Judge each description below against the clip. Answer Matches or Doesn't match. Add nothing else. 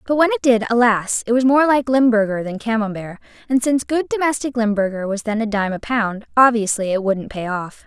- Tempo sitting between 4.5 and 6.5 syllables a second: Matches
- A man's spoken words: Doesn't match